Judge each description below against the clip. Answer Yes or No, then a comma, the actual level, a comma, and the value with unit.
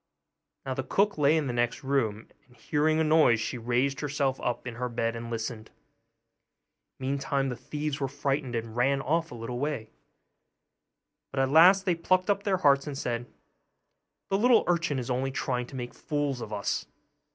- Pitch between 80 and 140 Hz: Yes, low, 135 Hz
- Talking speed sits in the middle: Yes, average, 185 wpm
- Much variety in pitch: No, average, 3.9 semitones